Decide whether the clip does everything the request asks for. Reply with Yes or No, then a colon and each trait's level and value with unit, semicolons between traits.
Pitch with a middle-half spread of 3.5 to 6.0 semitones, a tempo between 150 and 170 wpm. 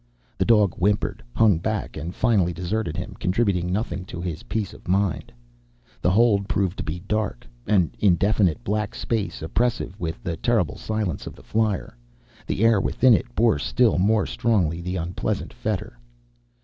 Yes: average, 3.9 semitones; average, 160 wpm